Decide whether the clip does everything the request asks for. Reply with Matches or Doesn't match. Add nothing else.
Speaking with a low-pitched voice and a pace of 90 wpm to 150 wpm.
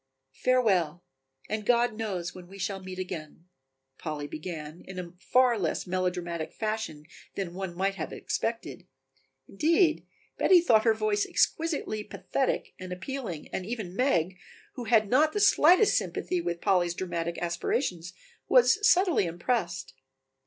Doesn't match